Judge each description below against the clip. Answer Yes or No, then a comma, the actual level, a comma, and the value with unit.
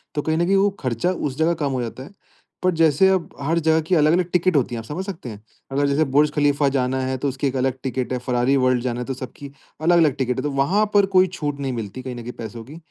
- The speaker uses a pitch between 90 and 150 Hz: Yes, medium, 140 Hz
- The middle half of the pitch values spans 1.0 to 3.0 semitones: No, average, 4.3 semitones